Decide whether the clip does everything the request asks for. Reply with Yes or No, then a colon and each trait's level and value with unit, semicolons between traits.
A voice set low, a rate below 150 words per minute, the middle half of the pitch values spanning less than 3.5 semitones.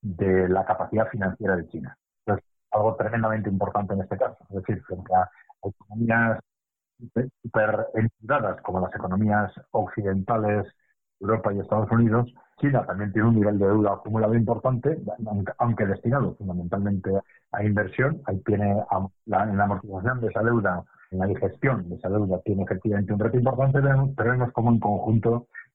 No: low, 105 Hz; average, 155 wpm; average, 3.0 semitones